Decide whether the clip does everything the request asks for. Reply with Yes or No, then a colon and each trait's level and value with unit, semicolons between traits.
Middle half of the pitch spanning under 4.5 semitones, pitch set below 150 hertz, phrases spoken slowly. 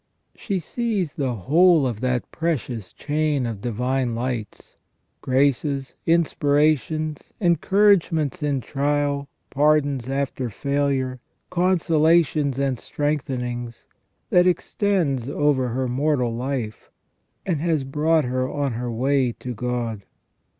Yes: average, 3.8 semitones; medium, 140 Hz; slow, 110 wpm